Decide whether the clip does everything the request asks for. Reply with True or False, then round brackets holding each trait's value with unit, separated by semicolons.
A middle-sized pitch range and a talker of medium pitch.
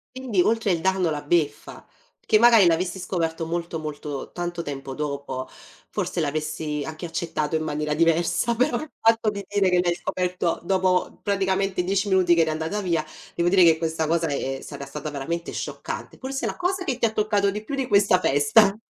True (4.2 semitones; 175 Hz)